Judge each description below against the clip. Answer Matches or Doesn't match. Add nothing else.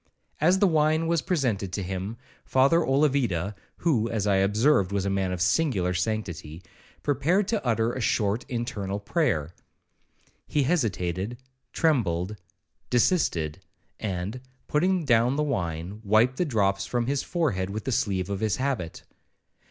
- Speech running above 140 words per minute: Doesn't match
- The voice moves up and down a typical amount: Doesn't match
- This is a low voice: Matches